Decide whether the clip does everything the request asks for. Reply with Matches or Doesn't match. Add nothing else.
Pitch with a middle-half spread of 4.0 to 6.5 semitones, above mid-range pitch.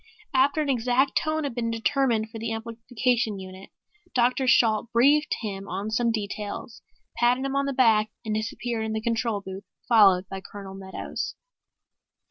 Doesn't match